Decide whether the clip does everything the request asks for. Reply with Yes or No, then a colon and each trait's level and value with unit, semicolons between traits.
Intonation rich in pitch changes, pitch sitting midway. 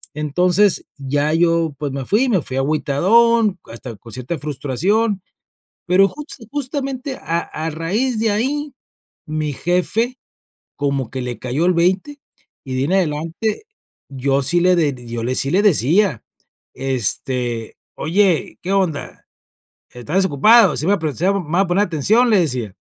Yes: wide, 6.7 semitones; medium, 170 Hz